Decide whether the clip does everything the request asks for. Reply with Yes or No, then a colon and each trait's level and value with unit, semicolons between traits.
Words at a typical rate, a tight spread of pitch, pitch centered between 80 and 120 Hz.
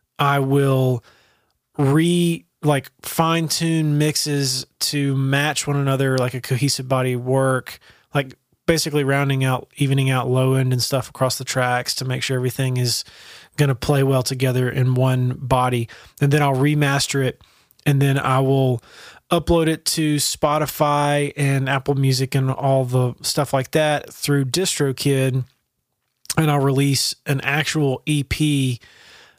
No: average, 145 wpm; narrow, 2.0 semitones; low, 135 Hz